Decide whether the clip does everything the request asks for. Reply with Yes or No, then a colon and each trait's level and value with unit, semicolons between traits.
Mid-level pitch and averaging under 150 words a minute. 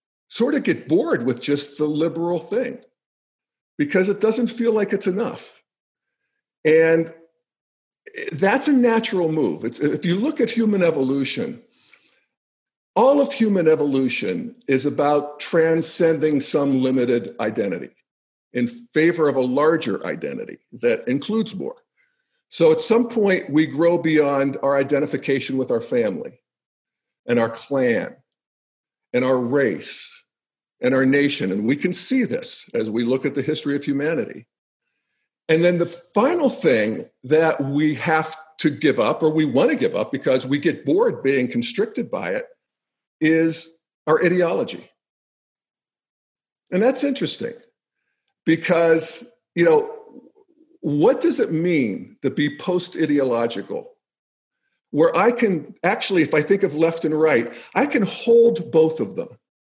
Yes: medium, 165 Hz; average, 140 wpm